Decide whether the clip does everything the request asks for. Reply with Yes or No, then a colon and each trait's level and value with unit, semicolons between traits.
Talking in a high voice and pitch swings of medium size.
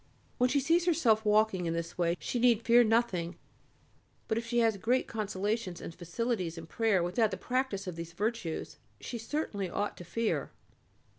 Yes: high, 220 Hz; average, 4.8 semitones